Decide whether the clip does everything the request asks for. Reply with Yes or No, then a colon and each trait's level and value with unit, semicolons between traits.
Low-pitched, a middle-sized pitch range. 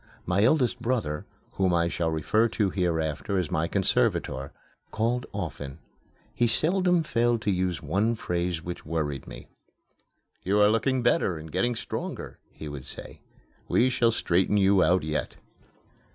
No: very low, 95 Hz; wide, 6.2 semitones